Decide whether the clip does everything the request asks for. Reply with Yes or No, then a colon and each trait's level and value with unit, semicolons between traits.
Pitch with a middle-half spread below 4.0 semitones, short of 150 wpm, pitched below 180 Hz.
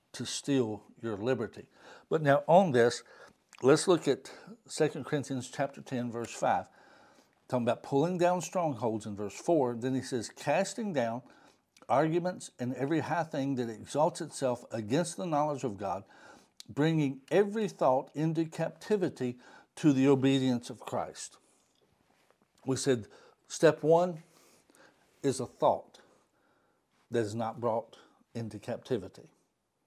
No: average, 4.9 semitones; slow, 135 wpm; low, 135 Hz